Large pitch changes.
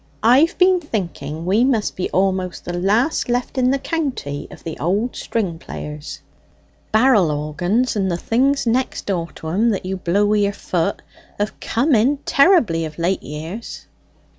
Yes: wide, 6.5 semitones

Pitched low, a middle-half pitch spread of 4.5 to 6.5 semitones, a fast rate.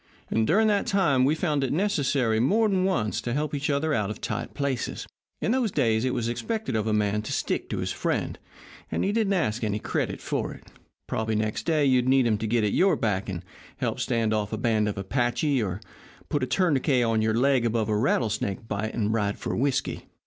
Yes: low, 120 Hz; average, 5.3 semitones; fast, 220 wpm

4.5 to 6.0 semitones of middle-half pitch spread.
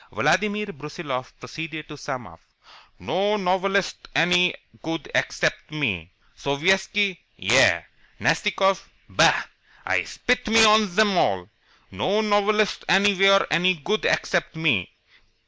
Yes: wide, 5.4 semitones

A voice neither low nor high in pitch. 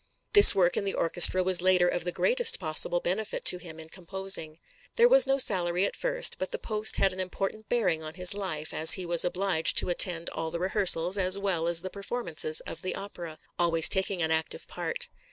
Yes: medium, 180 Hz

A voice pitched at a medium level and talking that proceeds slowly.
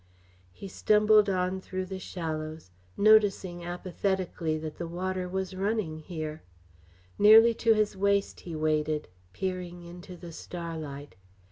Yes: medium, 180 Hz; slow, 125 wpm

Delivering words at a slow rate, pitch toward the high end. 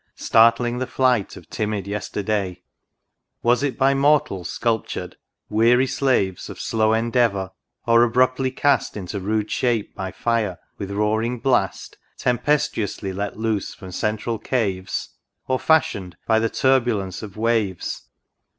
No: slow, 130 wpm; low, 110 Hz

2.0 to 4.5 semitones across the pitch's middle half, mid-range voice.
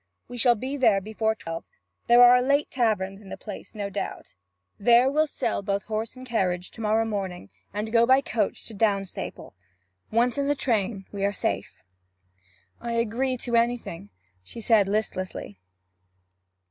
No: average, 3.5 semitones; high, 220 Hz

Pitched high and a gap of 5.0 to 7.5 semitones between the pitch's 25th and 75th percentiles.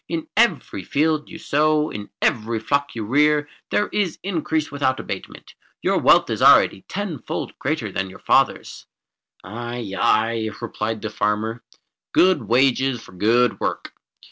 No: low, 130 Hz; wide, 5.5 semitones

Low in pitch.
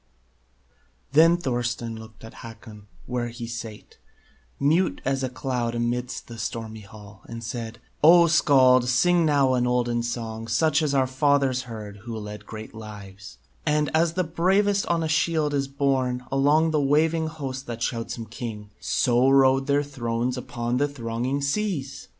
Yes: low, 125 Hz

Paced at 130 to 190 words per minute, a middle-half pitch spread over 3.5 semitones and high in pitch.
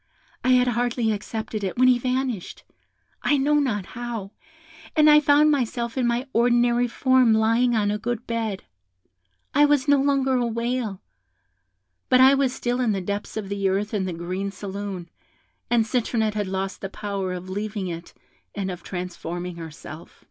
Yes: average, 170 wpm; average, 4.3 semitones; high, 225 Hz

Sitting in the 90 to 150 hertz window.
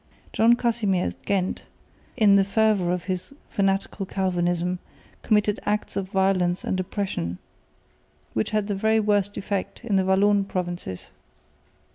No: high, 195 Hz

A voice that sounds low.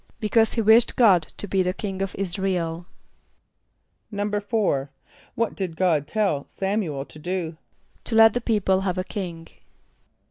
No: high, 190 Hz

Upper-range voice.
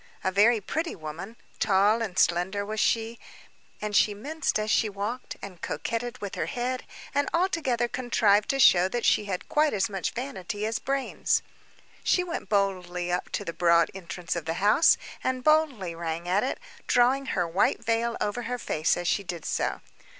Yes: high, 210 Hz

